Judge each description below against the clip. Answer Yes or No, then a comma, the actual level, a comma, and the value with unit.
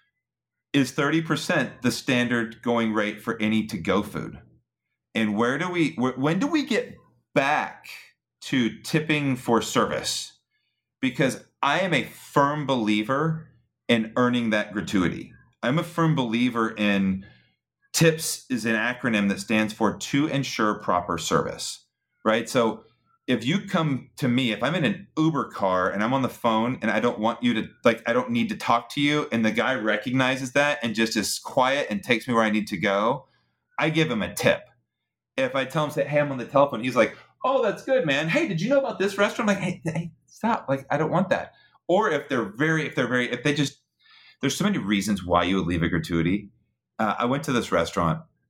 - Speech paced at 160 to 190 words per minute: No, fast, 205 wpm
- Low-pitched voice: Yes, low, 130 Hz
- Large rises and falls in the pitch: Yes, wide, 6.1 semitones